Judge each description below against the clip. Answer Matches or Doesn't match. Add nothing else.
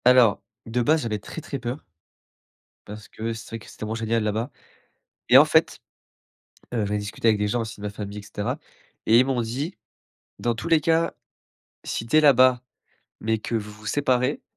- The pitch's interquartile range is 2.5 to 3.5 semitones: Matches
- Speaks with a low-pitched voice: Matches